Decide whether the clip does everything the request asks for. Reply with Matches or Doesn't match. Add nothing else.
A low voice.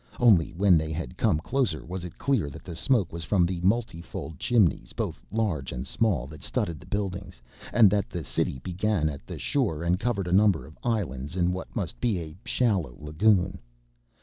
Matches